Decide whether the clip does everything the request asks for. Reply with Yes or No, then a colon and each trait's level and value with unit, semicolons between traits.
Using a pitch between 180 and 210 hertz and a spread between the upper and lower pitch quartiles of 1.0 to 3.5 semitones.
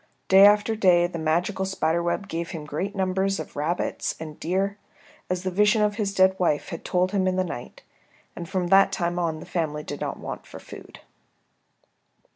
Yes: medium, 185 Hz; narrow, 2.6 semitones